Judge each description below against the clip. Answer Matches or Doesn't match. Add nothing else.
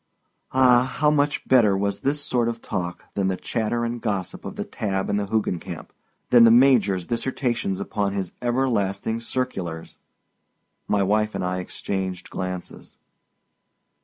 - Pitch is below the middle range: Matches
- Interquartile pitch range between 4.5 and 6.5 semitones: Doesn't match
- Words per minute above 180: Doesn't match